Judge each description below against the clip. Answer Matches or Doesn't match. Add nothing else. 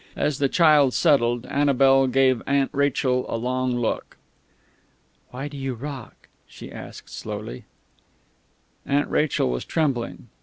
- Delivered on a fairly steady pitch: Matches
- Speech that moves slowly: Matches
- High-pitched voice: Doesn't match